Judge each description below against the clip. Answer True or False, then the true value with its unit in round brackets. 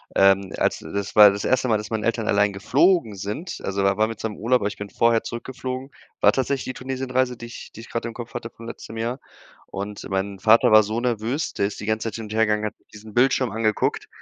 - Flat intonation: False (3.0 semitones)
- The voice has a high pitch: False (110 Hz)